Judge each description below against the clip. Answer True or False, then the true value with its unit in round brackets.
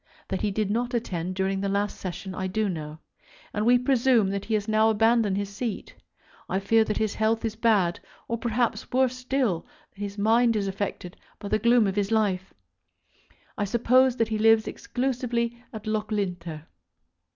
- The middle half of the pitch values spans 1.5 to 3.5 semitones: True (3.1 semitones)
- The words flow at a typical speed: True (180 wpm)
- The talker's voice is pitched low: False (215 Hz)